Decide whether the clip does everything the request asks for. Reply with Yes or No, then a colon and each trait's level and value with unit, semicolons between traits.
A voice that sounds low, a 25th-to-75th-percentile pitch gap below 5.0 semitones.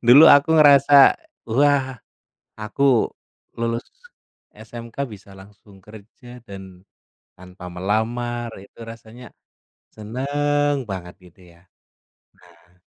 No: low, 115 Hz; average, 5.3 semitones